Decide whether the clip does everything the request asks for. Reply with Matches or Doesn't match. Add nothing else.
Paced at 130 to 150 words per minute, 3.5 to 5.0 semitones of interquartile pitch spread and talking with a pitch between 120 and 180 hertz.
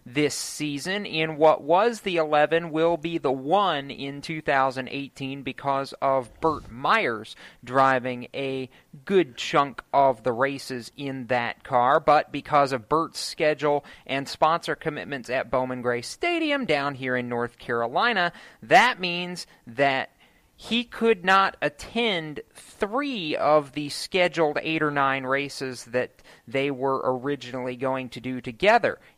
Matches